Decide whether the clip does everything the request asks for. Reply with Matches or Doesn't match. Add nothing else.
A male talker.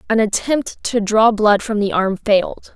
Doesn't match